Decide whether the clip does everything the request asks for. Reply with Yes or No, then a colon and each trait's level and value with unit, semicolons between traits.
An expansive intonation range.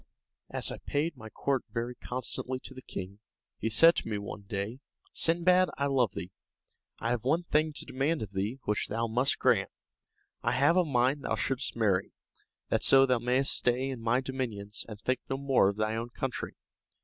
No: average, 3.8 semitones